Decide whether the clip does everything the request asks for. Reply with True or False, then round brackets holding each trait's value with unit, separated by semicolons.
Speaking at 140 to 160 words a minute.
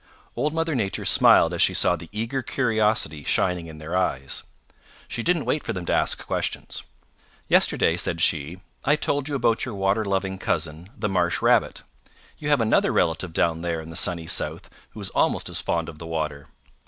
False (190 wpm)